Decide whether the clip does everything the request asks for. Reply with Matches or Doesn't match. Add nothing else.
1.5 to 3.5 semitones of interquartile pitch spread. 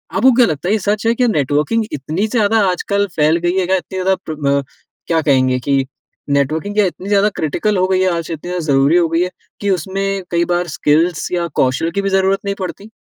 Doesn't match